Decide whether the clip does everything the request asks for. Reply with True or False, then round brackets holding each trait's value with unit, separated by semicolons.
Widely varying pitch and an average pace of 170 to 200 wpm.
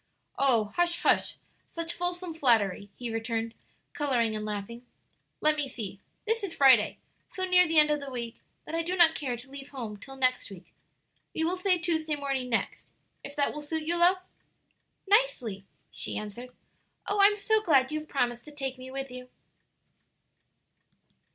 True (5.8 semitones; 175 wpm)